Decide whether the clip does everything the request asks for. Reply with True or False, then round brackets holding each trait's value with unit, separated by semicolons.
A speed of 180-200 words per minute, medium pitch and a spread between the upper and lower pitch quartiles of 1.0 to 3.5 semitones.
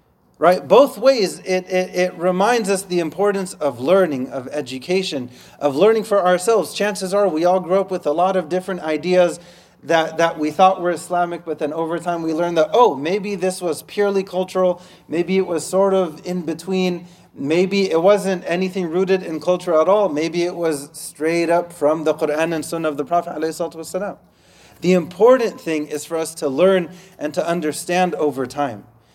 True (185 wpm; 175 Hz; 2.9 semitones)